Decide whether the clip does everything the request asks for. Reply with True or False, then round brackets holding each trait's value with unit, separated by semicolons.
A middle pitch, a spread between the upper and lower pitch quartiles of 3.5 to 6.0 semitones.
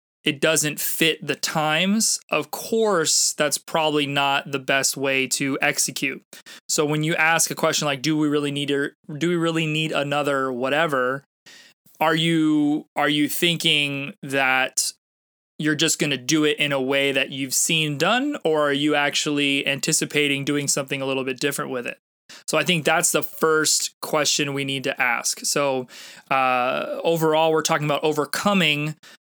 False (150 Hz; 2.4 semitones)